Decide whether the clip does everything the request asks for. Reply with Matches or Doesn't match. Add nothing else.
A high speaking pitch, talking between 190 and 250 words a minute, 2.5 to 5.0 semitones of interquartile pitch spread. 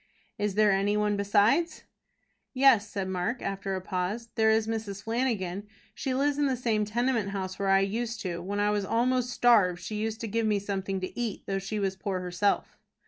Matches